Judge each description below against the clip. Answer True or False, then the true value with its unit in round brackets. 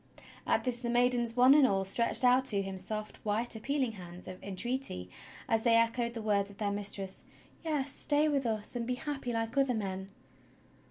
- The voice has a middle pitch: False (230 Hz)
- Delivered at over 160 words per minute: True (200 wpm)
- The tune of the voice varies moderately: True (3.9 semitones)